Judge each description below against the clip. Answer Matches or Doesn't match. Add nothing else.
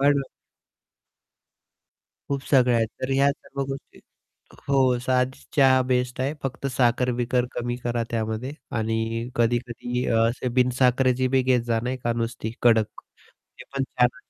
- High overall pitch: Doesn't match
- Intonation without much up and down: Matches